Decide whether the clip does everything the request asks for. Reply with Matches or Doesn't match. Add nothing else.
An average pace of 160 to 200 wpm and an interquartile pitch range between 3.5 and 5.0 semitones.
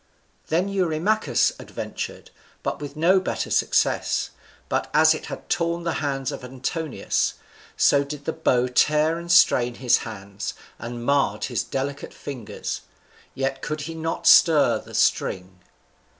Doesn't match